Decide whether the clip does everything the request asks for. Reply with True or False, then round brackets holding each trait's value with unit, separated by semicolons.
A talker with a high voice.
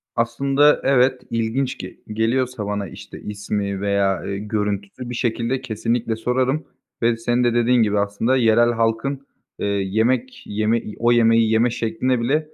False (115 Hz)